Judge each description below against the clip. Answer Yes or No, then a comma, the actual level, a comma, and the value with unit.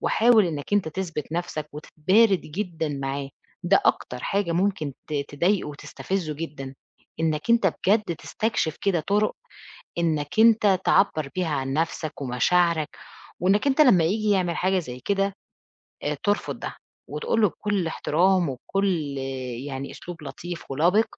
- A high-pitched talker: No, medium, 175 Hz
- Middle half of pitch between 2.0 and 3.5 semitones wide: No, average, 4.8 semitones